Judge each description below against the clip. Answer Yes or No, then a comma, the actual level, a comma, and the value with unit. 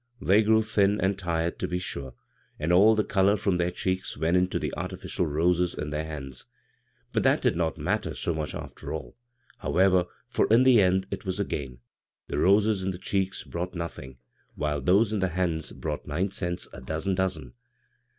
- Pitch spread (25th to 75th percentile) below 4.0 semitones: Yes, average, 3.4 semitones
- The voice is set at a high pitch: No, very low, 90 Hz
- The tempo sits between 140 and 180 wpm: No, average, 200 wpm